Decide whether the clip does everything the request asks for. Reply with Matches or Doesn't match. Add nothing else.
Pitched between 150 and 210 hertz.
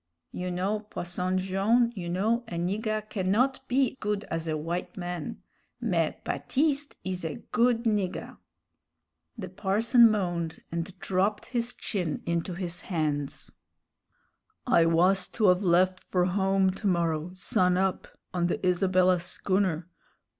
Matches